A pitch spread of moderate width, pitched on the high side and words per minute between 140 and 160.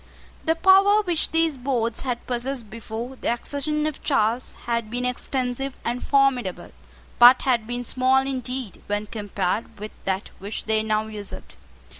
Yes: average, 3.8 semitones; high, 245 Hz; average, 150 wpm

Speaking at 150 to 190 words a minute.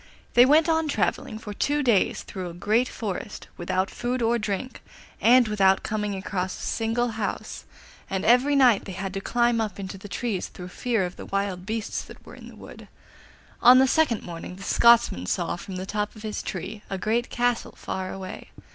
No: average, 200 wpm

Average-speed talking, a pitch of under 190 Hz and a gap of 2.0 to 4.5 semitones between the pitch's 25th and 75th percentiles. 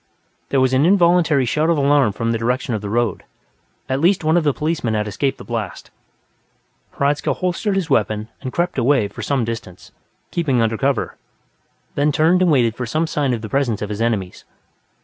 No: average, 195 wpm; low, 135 Hz; average, 5.3 semitones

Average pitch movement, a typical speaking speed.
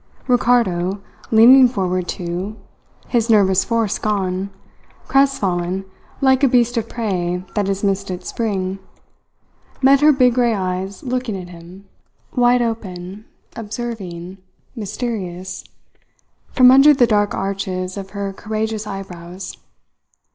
No: average, 4.4 semitones; slow, 120 wpm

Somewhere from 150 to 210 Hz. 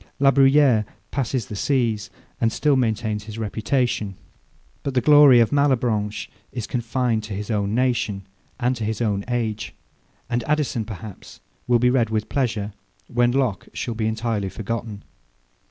No: low, 115 Hz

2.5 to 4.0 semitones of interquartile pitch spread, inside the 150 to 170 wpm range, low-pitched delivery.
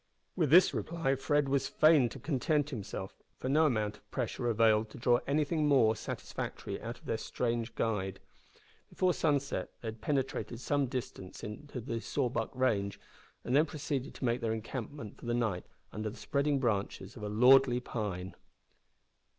No: average, 4.4 semitones; average, 165 wpm; low, 125 Hz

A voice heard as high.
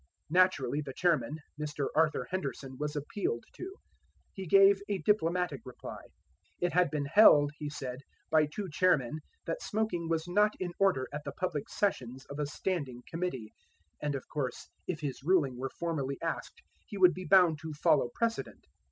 No: medium, 155 Hz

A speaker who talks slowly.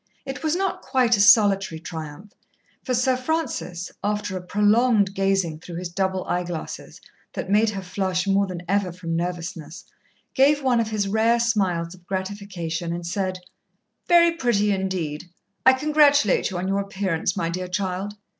No: average, 165 wpm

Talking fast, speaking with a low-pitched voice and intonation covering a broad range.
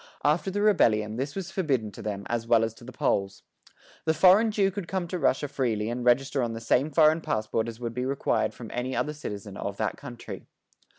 Yes: fast, 220 wpm; low, 130 Hz; wide, 6.2 semitones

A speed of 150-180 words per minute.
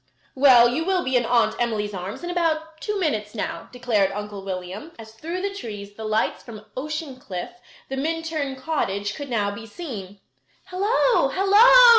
Yes: average, 170 wpm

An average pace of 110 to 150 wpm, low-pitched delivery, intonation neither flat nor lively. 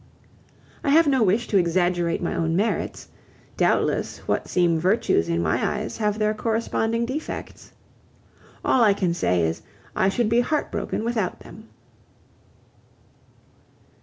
No: slow, 135 wpm; high, 210 Hz; average, 5.0 semitones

